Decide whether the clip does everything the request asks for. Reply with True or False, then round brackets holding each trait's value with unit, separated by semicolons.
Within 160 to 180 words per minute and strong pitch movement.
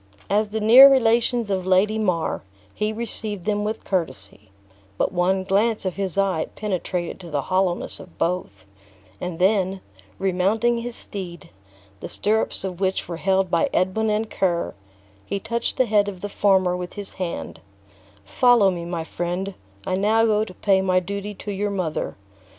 False (165 wpm; 2.9 semitones)